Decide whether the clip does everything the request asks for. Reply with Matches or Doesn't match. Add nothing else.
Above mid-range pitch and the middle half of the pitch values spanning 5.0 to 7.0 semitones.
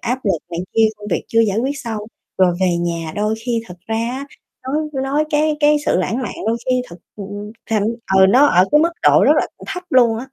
Matches